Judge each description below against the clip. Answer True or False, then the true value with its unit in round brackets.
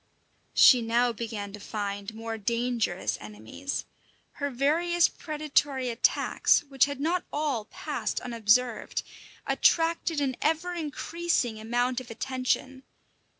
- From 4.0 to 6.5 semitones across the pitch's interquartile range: True (4.6 semitones)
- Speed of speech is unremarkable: False (110 wpm)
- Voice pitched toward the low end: False (250 Hz)